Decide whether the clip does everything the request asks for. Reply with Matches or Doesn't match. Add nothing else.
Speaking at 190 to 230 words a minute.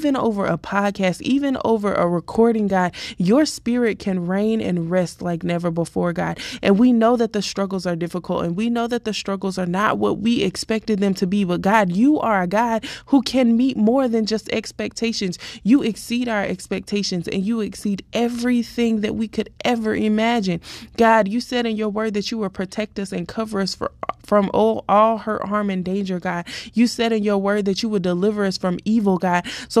Matches